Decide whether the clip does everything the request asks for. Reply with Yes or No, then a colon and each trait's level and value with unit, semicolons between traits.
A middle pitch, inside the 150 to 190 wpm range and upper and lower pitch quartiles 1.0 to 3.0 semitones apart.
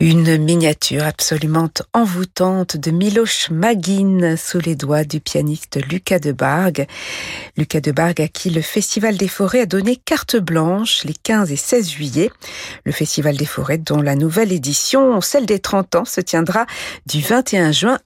No: medium, 175 Hz; average, 165 wpm; average, 5.2 semitones